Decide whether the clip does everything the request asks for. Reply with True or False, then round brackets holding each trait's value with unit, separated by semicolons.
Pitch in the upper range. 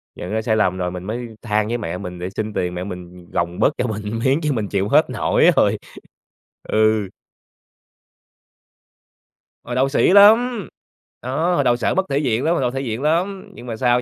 False (115 Hz)